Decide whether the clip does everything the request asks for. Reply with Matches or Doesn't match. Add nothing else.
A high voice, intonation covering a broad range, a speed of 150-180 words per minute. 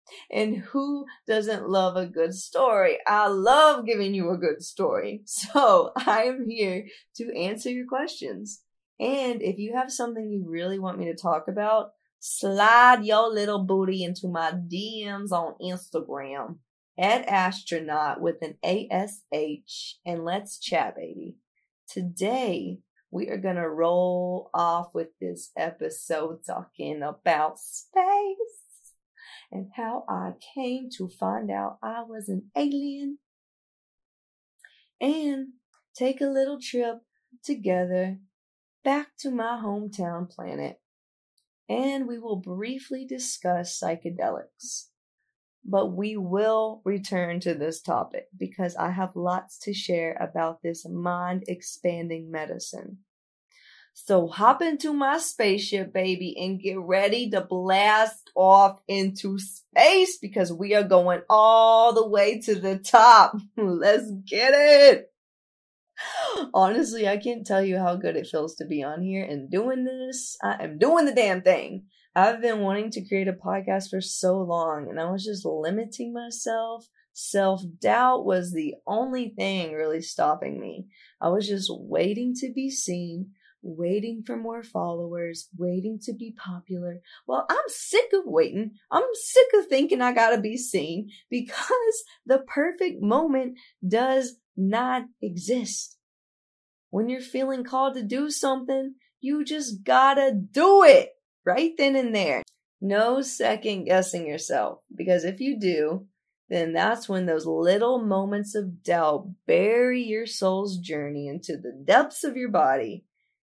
Doesn't match